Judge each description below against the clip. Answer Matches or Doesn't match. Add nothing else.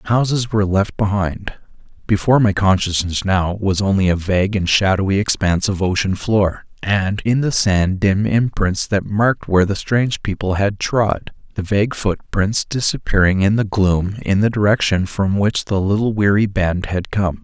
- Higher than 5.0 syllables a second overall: Doesn't match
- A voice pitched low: Matches